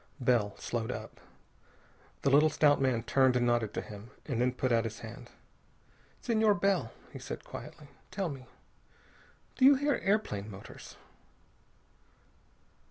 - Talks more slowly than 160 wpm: Yes, average, 140 wpm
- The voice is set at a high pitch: No, low, 130 Hz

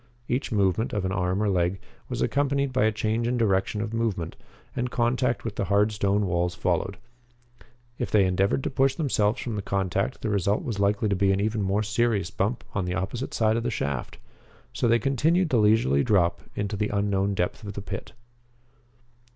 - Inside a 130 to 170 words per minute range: No, average, 200 wpm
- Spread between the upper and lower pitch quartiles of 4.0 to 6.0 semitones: No, average, 3.1 semitones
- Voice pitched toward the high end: No, low, 105 Hz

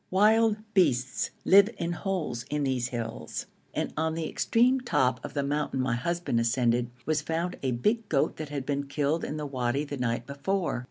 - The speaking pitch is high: No, medium, 145 Hz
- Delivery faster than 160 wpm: Yes, average, 185 wpm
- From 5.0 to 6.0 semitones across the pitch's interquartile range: Yes, wide, 5.5 semitones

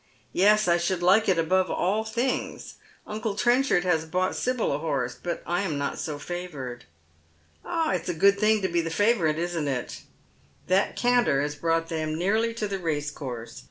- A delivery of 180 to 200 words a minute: Yes, average, 195 wpm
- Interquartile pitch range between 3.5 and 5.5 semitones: Yes, average, 5.1 semitones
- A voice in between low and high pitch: Yes, medium, 175 Hz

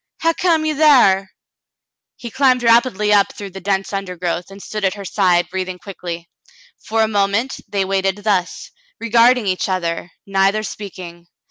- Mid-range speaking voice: No, high, 195 Hz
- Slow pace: No, average, 155 wpm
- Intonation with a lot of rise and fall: No, average, 3.6 semitones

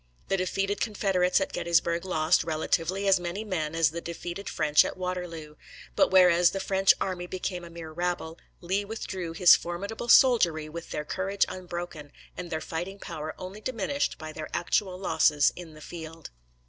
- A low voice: No, medium, 175 Hz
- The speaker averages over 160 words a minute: Yes, average, 170 wpm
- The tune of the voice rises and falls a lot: No, average, 2.7 semitones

